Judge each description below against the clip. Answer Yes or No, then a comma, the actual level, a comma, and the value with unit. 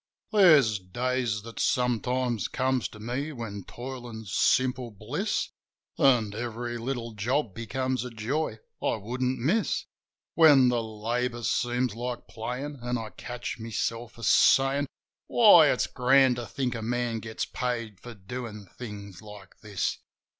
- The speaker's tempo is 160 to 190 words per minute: No, average, 140 wpm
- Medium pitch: No, low, 120 Hz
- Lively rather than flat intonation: No, narrow, 2.6 semitones